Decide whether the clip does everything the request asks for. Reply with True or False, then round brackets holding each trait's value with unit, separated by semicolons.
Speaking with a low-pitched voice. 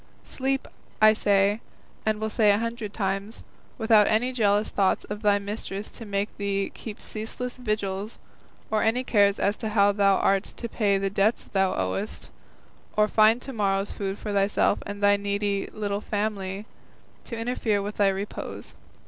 False (205 Hz)